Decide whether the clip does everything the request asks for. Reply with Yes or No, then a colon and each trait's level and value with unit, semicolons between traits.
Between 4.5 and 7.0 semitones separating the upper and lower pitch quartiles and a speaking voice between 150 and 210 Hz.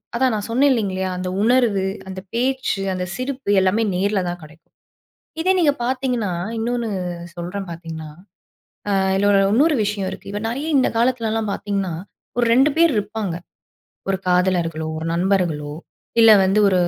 Yes: average, 4.9 semitones; high, 205 Hz